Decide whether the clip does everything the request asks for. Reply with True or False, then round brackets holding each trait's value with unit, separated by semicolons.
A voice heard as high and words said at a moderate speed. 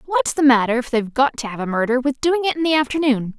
False (265 Hz; 285 wpm)